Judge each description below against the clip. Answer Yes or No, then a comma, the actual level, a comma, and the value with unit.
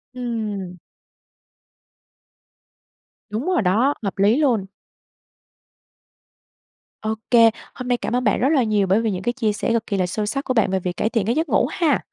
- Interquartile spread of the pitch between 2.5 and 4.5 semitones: Yes, average, 3.7 semitones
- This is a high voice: Yes, high, 225 Hz